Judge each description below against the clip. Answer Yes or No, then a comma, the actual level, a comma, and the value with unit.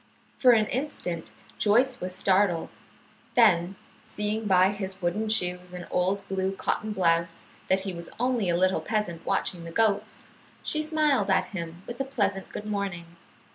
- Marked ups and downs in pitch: No, average, 3.4 semitones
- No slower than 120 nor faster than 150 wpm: No, average, 160 wpm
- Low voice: No, high, 195 Hz